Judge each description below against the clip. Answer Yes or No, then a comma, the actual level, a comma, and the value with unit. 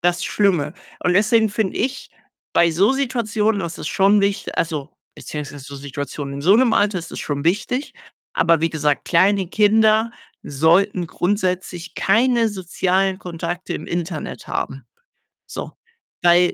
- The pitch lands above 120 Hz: Yes, medium, 185 Hz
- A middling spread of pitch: Yes, average, 4.2 semitones